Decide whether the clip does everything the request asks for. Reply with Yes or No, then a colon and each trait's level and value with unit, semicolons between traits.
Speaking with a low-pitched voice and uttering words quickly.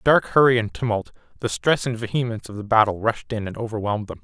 Yes: low, 115 Hz; fast, 240 wpm